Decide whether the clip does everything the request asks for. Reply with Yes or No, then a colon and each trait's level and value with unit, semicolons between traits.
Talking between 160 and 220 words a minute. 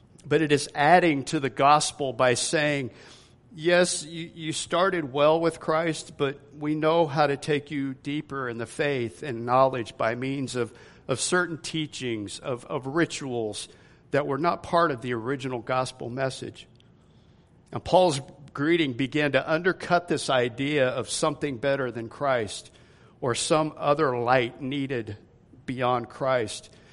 No: average, 145 wpm